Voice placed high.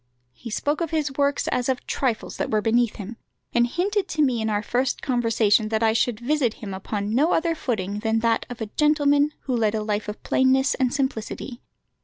Yes: high, 240 Hz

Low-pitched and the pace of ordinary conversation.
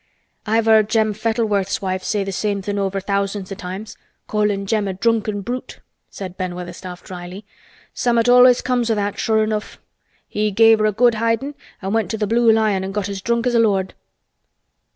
No: high, 210 Hz; average, 190 wpm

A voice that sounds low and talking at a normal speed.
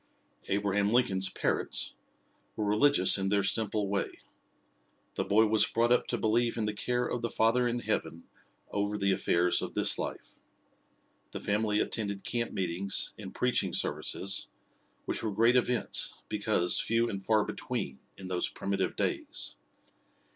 Yes: low, 105 Hz; average, 150 wpm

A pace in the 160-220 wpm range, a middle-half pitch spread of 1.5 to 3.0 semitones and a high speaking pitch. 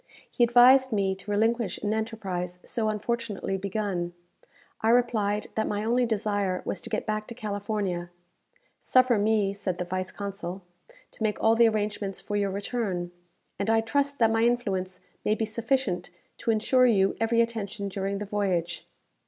Yes: average, 165 wpm; average, 2.7 semitones; high, 210 Hz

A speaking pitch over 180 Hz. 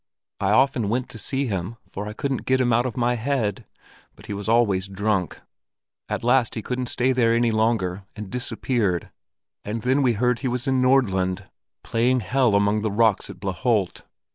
No: low, 115 Hz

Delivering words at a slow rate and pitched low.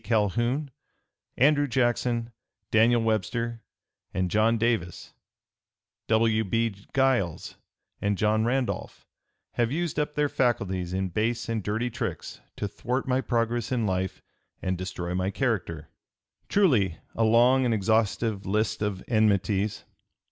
Yes: slow, 125 wpm; low, 115 Hz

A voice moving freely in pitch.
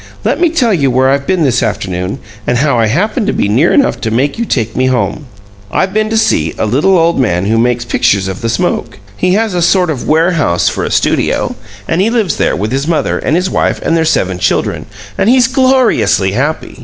Yes: wide, 8.8 semitones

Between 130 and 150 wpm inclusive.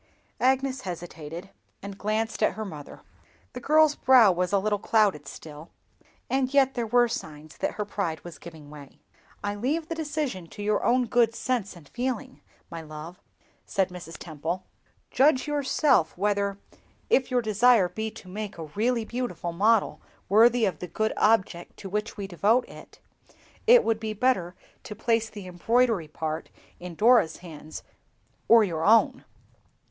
No: average, 160 wpm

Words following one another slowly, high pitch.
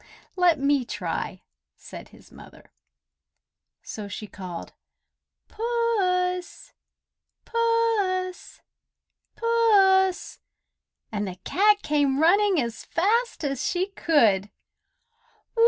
Yes: slow, 85 wpm; very high, 365 Hz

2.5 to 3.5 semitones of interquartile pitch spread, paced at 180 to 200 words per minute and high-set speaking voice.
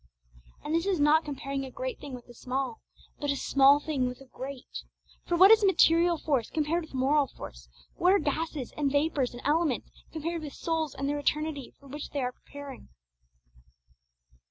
Yes: average, 3.1 semitones; average, 185 wpm; very high, 290 Hz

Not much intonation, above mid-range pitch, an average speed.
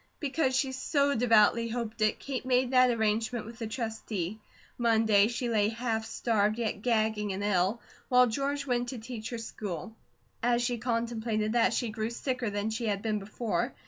Yes: narrow, 2.2 semitones; high, 230 Hz; average, 175 wpm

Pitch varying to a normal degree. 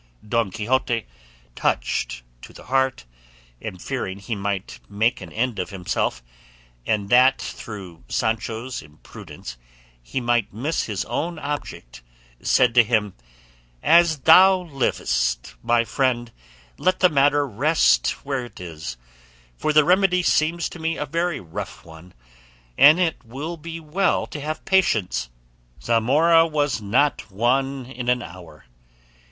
No: wide, 7.0 semitones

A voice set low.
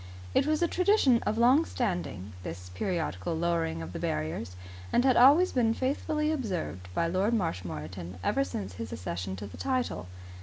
No: medium, 170 Hz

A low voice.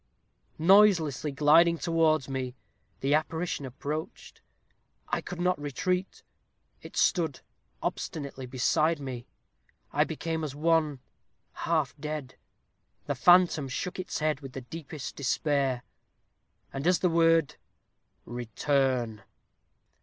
No: medium, 150 Hz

